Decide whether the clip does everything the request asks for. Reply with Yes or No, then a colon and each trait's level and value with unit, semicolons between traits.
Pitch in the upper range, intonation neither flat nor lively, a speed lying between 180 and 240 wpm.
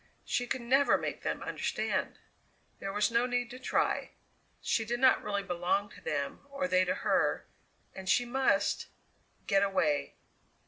No: high, 210 Hz; average, 4.3 semitones; average, 155 wpm